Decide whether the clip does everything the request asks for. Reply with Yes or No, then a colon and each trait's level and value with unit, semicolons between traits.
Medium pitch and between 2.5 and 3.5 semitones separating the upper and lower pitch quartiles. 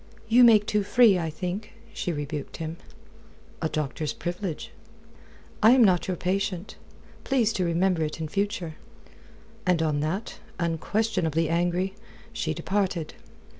No: medium, 180 Hz; average, 4.1 semitones